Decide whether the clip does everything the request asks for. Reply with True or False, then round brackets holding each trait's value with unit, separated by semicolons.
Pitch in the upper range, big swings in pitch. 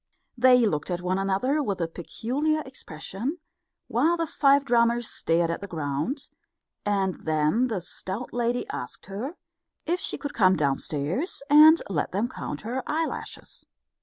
True (225 Hz; 7.7 semitones)